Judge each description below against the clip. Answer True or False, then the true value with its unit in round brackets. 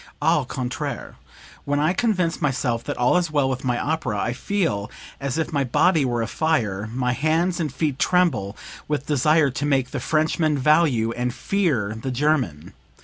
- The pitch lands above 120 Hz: True (140 Hz)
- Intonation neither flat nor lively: True (4.5 semitones)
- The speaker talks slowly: False (170 wpm)